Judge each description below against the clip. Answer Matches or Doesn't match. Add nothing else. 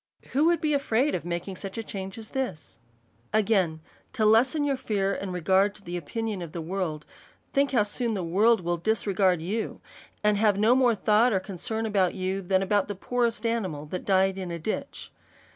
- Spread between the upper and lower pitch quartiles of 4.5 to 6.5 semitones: Doesn't match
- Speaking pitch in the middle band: Doesn't match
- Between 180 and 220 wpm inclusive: Matches